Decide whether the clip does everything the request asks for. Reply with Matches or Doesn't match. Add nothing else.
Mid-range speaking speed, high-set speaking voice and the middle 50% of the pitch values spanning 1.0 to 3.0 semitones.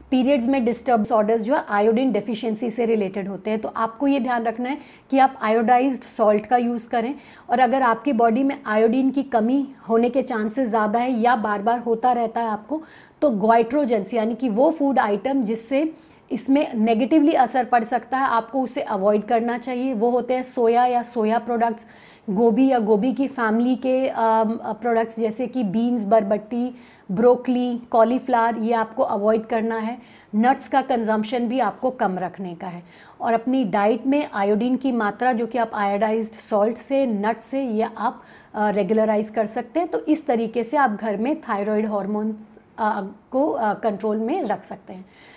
Matches